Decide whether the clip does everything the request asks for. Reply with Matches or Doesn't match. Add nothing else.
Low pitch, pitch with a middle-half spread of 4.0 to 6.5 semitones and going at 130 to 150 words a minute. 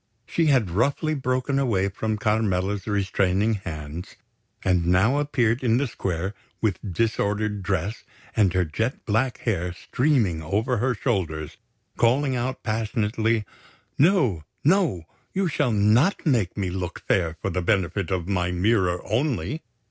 Matches